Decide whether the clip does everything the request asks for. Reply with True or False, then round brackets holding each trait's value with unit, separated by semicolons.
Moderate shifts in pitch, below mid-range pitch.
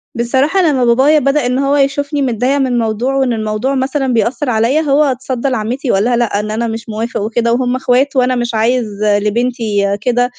False (3.1 semitones; 245 Hz)